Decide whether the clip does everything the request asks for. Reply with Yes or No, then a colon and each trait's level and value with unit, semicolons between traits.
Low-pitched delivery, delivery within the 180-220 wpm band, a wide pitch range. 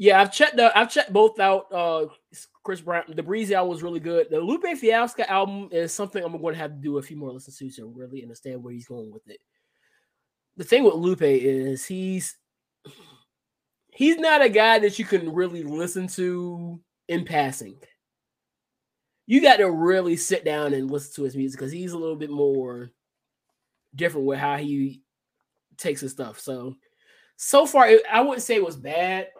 No: medium, 170 Hz; average, 195 wpm; wide, 7.0 semitones